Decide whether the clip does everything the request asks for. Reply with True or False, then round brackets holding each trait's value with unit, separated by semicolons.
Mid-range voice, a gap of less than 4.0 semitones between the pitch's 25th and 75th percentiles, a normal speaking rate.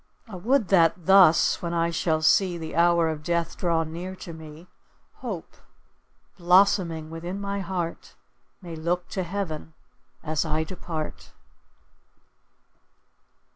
False (170 Hz; 2.4 semitones; 125 wpm)